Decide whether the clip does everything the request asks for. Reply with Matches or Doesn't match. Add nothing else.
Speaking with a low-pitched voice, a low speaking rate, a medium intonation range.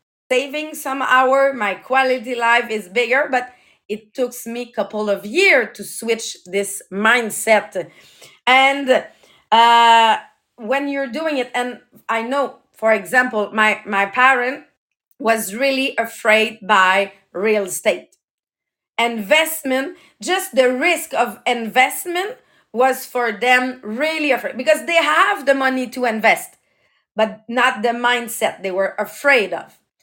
Doesn't match